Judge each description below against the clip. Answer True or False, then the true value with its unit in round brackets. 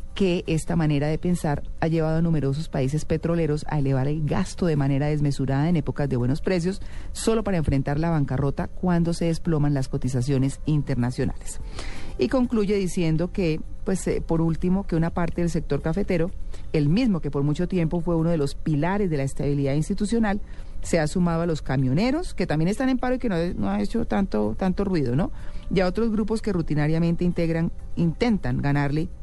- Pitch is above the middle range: False (165 Hz)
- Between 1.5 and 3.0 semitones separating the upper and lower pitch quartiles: False (4.4 semitones)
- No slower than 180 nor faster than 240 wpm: True (190 wpm)